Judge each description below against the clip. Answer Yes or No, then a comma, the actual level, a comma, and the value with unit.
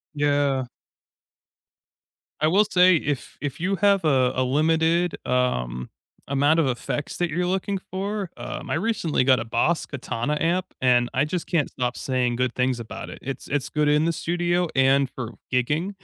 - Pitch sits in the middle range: Yes, medium, 145 Hz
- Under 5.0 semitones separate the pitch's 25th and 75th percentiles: No, average, 5.3 semitones